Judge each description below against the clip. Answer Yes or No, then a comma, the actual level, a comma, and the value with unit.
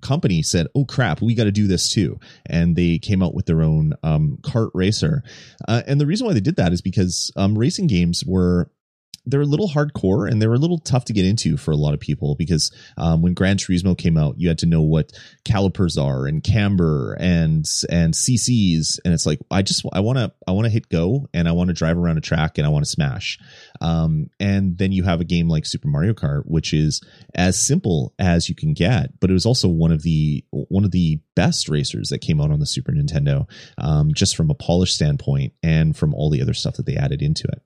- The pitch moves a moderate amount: No, wide, 8.2 semitones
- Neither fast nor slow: No, fast, 240 wpm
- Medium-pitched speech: No, very low, 95 Hz